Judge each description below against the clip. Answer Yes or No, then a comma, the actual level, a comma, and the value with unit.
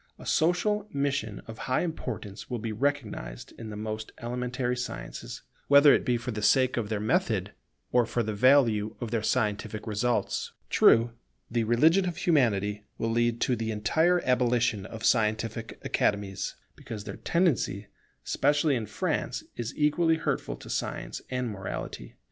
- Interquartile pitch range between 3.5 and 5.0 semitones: Yes, average, 4.4 semitones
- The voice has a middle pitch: No, low, 120 Hz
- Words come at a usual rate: Yes, average, 155 wpm